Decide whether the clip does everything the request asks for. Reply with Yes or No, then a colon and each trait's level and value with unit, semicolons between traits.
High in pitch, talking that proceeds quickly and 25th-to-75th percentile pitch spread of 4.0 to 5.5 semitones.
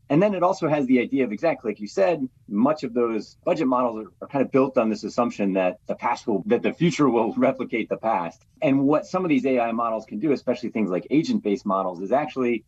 No: low, 120 Hz; fast, 250 wpm; average, 4.7 semitones